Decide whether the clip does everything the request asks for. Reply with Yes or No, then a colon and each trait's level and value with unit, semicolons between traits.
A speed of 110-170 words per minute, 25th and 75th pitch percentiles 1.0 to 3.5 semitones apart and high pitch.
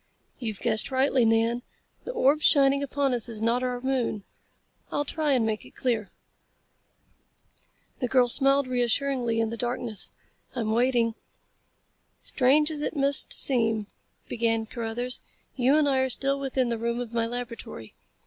Yes: average, 150 wpm; average, 2.9 semitones; high, 245 Hz